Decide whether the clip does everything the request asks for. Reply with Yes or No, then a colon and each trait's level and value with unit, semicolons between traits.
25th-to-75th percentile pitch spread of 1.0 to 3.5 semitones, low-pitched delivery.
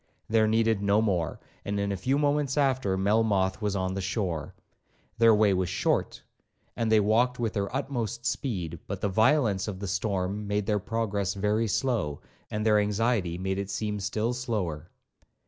Yes: average, 2.9 semitones; low, 105 Hz